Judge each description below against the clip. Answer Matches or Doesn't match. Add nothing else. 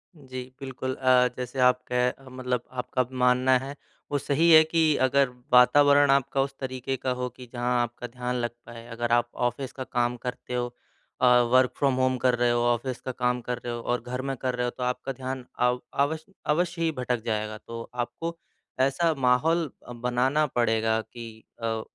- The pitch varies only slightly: Matches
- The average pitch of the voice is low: Matches